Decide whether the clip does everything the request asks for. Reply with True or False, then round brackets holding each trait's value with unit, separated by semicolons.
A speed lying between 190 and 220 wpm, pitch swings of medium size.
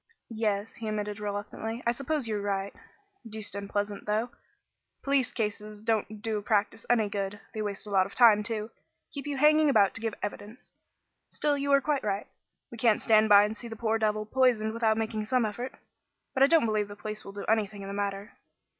False (205 wpm; 2.2 semitones)